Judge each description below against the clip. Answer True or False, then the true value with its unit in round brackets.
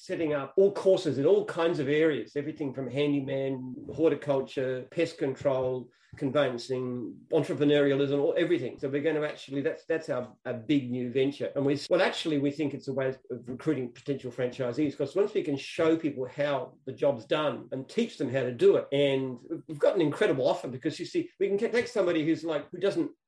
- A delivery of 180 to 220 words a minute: True (200 wpm)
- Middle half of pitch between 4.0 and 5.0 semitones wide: False (3.3 semitones)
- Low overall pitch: False (145 Hz)